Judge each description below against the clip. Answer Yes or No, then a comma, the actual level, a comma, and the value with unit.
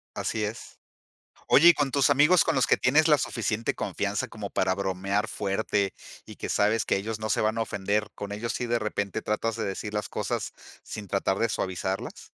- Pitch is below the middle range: Yes, low, 105 Hz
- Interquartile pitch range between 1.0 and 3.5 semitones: Yes, average, 2.8 semitones